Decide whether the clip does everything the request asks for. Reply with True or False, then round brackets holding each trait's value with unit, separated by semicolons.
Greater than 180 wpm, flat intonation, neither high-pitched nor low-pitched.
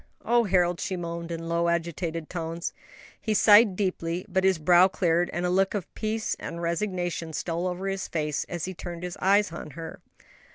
True (190 wpm; 2.2 semitones; 175 Hz)